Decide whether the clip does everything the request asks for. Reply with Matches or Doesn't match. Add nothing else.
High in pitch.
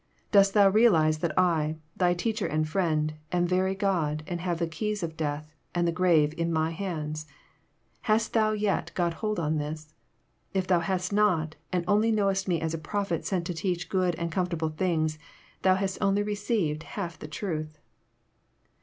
Doesn't match